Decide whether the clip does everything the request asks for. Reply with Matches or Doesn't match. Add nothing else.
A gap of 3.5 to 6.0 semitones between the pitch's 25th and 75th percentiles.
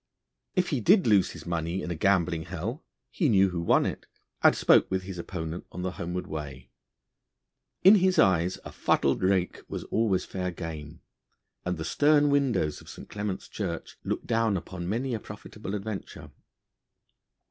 Matches